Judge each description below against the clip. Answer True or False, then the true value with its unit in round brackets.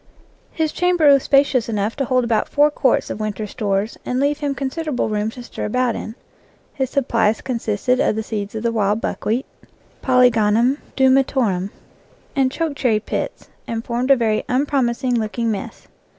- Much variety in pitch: False (3.8 semitones)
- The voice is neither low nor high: False (245 Hz)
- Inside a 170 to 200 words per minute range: True (175 wpm)